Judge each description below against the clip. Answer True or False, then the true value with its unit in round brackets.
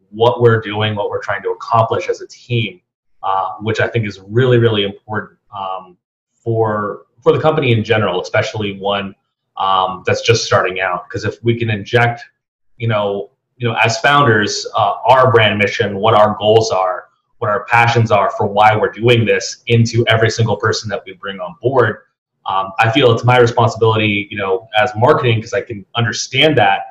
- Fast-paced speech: False (190 wpm)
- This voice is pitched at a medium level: False (115 Hz)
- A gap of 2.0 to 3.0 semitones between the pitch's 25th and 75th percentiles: True (2.7 semitones)